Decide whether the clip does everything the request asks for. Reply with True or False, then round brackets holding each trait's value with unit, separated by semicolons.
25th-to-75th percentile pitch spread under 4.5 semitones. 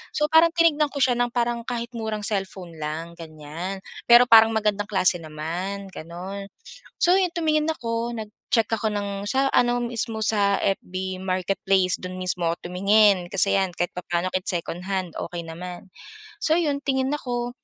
False (4.8 semitones)